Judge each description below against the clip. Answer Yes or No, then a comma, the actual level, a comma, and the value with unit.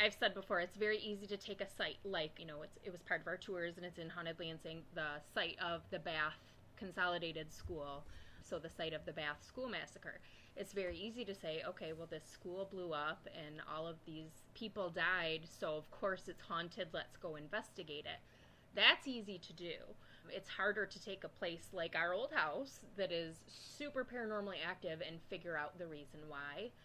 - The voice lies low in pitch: No, medium, 175 Hz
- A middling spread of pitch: Yes, average, 3.6 semitones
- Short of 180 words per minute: No, fast, 205 wpm